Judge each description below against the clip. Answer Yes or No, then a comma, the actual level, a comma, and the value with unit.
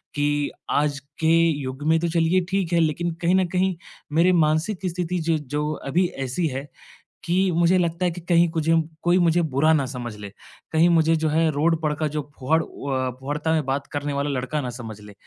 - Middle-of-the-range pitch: Yes, medium, 160 Hz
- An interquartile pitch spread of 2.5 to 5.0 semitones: Yes, average, 2.9 semitones